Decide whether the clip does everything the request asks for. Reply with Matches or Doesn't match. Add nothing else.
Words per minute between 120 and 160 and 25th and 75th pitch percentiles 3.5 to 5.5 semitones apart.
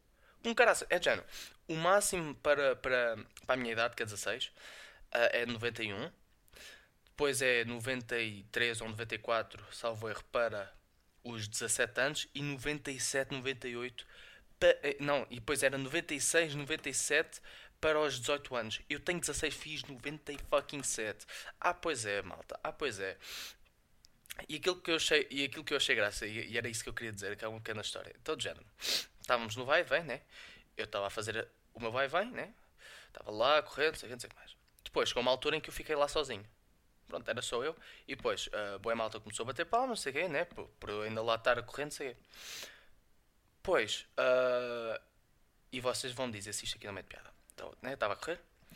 Doesn't match